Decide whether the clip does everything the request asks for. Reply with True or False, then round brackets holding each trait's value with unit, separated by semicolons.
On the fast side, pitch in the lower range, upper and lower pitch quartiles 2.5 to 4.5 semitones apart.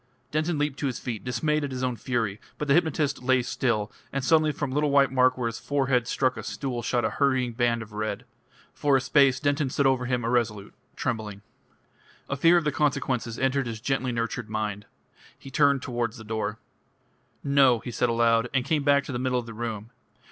True (215 wpm; 130 Hz; 3.2 semitones)